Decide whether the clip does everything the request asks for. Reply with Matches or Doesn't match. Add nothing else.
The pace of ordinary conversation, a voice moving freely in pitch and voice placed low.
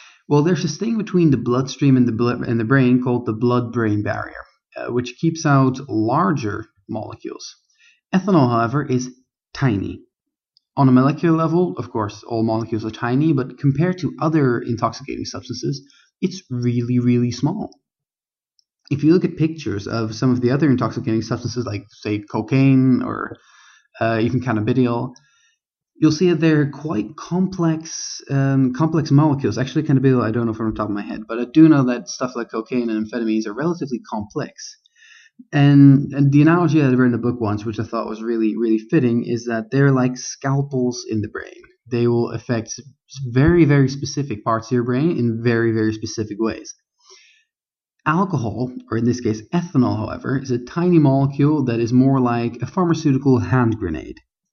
Doesn't match